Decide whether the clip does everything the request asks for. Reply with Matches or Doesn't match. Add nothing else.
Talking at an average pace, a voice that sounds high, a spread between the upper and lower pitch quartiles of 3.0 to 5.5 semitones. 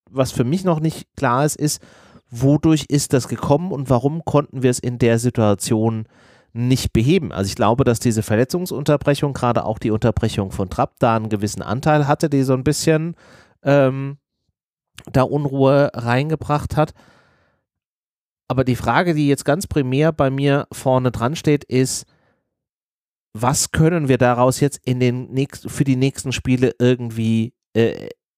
Doesn't match